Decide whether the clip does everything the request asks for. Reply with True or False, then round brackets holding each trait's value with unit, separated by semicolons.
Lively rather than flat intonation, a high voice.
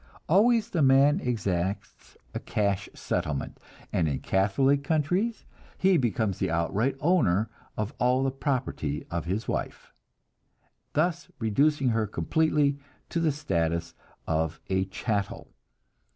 False (7.6 semitones; 120 Hz)